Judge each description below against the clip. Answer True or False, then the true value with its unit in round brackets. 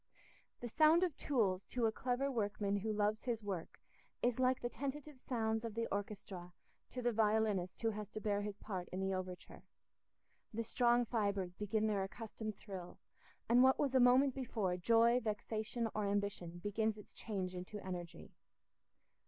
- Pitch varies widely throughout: False (3.3 semitones)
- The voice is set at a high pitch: True (215 Hz)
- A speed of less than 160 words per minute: False (170 wpm)